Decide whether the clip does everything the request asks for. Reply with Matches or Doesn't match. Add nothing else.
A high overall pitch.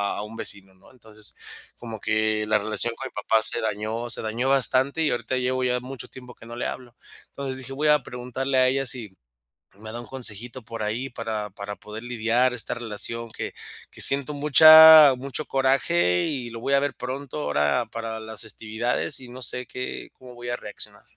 Doesn't match